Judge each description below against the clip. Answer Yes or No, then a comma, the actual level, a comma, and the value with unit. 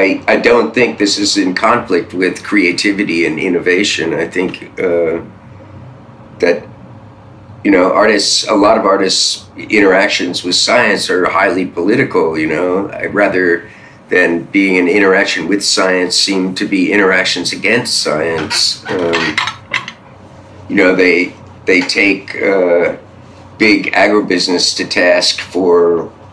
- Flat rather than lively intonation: No, average, 3.1 semitones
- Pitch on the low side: Yes, very low, 95 Hz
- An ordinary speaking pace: No, slow, 130 wpm